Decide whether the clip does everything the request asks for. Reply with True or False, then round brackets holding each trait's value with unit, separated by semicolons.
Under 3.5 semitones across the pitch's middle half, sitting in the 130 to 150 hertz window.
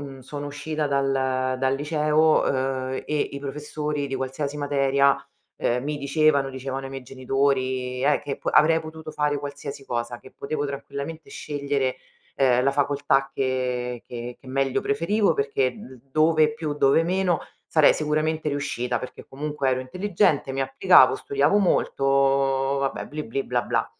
True (2.4 semitones; 140 Hz)